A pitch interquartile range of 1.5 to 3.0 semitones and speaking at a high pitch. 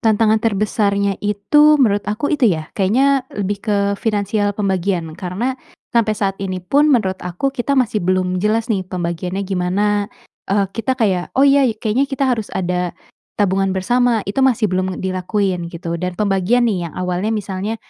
No: average, 3.6 semitones; high, 205 Hz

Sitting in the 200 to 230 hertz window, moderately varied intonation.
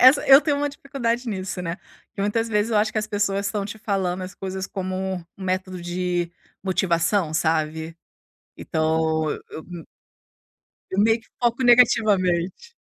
No: high, 190 Hz; average, 4.3 semitones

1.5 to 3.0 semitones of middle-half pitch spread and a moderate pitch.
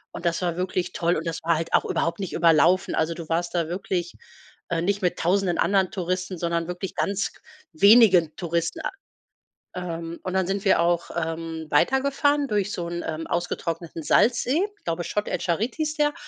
Yes: average, 2.7 semitones; medium, 175 Hz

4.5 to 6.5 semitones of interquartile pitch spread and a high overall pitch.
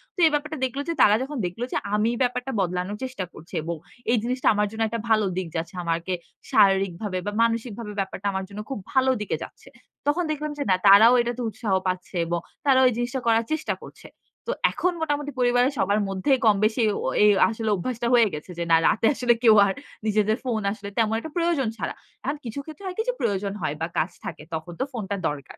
Yes: average, 4.8 semitones; high, 220 Hz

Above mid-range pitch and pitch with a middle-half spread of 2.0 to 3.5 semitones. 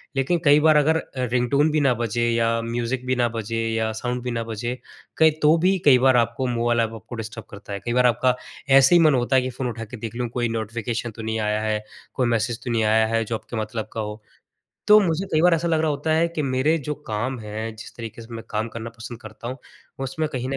No: low, 120 Hz; average, 3.2 semitones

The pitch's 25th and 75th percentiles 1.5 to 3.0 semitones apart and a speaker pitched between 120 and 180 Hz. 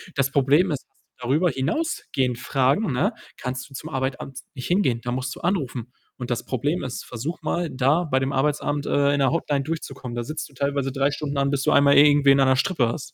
Yes: narrow, 2.5 semitones; medium, 140 Hz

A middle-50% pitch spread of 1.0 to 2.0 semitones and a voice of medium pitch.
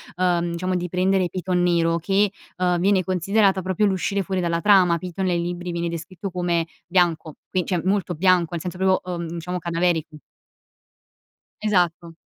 Yes: narrow, 1.6 semitones; medium, 180 Hz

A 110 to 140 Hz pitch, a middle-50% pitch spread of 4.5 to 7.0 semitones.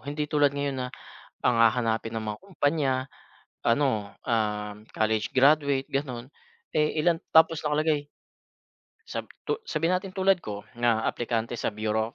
Yes: low, 135 Hz; average, 5.3 semitones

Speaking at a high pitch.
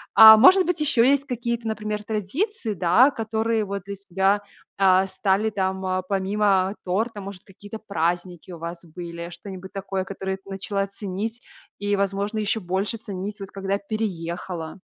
Yes: high, 200 Hz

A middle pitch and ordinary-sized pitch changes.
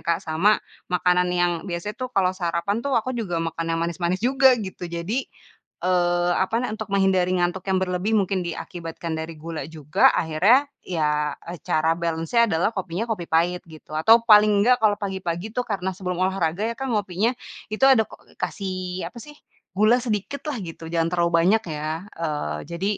Yes: medium, 180 Hz; average, 3.9 semitones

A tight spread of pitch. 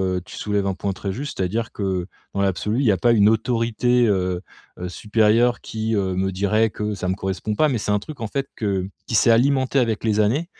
No: average, 3.4 semitones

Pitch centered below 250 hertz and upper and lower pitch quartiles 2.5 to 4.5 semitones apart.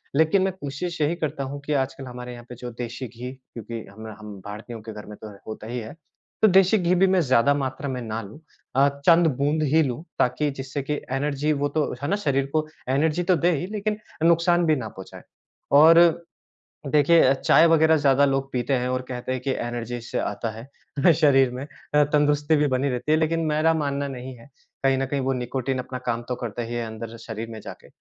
Yes: low, 135 Hz; average, 4.0 semitones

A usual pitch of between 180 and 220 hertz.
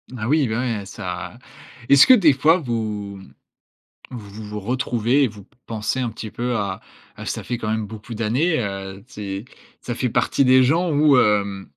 No: low, 115 Hz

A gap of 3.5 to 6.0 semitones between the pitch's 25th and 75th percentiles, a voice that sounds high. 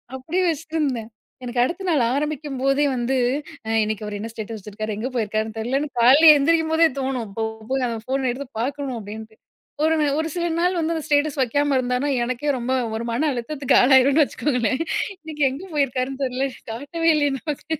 Yes: average, 4.0 semitones; very high, 270 Hz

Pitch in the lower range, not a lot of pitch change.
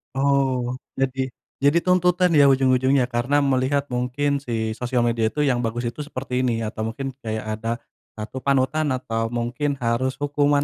No: low, 130 Hz; average, 3.0 semitones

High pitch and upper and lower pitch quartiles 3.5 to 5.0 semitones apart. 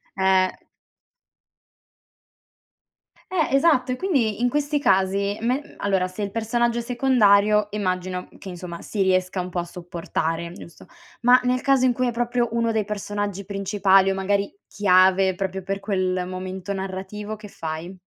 Yes: high, 200 Hz; average, 4.0 semitones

